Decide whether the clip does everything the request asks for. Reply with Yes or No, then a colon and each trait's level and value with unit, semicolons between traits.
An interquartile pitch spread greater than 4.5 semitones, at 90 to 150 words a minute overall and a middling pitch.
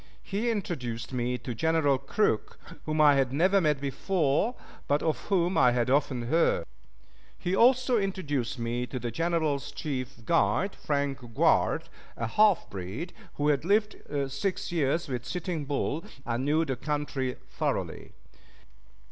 Yes: wide, 5.4 semitones; average, 145 wpm; medium, 145 Hz